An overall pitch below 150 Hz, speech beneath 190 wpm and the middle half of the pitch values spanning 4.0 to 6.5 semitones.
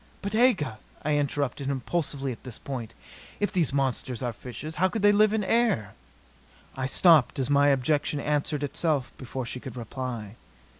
Yes: medium, 140 Hz; average, 180 wpm; average, 4.3 semitones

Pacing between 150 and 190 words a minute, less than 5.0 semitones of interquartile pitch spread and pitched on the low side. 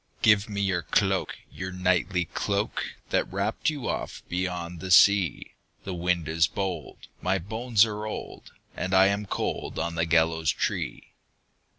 Yes: average, 155 wpm; average, 2.9 semitones; very low, 95 Hz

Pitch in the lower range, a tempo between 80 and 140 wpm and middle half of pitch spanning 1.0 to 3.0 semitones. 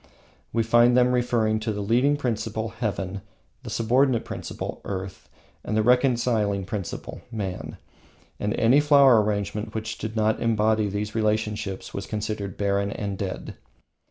Yes: low, 110 Hz; slow, 135 wpm; narrow, 2.5 semitones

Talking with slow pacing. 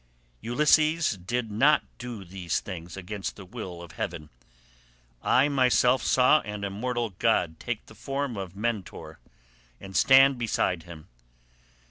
Yes: slow, 130 wpm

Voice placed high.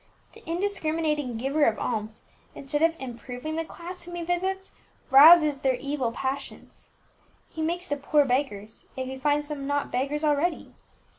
Yes: very high, 290 Hz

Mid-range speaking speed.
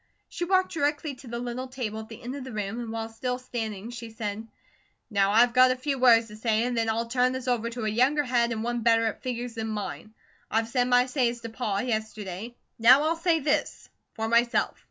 No: fast, 235 wpm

